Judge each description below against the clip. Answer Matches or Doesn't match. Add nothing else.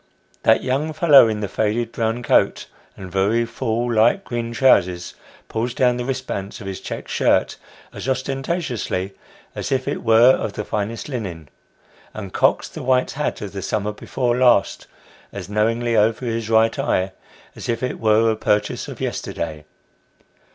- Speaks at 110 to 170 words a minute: Matches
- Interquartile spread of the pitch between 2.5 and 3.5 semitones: Matches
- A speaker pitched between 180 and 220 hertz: Doesn't match